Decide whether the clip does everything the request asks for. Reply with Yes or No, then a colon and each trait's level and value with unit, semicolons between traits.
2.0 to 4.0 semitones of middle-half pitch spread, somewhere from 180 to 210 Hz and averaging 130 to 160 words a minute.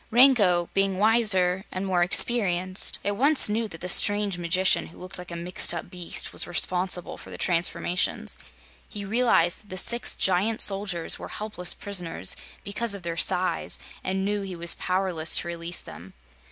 No: average, 2.7 semitones; medium, 185 Hz; average, 175 wpm